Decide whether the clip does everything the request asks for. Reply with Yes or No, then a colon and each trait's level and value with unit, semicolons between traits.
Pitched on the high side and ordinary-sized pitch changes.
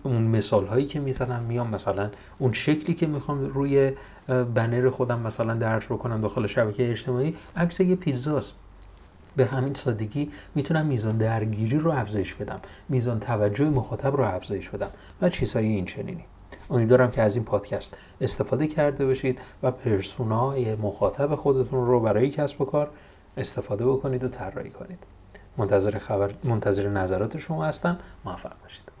No: low, 125 Hz; average, 4.6 semitones